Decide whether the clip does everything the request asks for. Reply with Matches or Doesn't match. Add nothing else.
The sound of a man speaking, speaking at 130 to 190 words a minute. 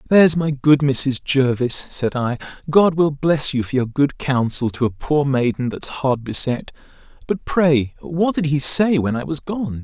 Doesn't match